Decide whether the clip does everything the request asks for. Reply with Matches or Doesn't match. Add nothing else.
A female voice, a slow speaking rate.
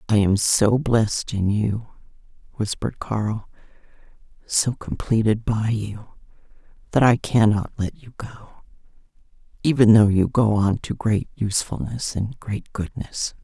Matches